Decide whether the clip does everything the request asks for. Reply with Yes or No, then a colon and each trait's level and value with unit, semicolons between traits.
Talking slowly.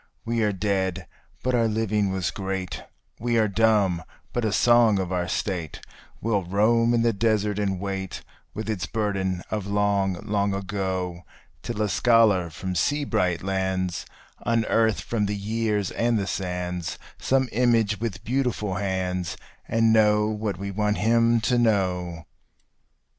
No: average, 150 wpm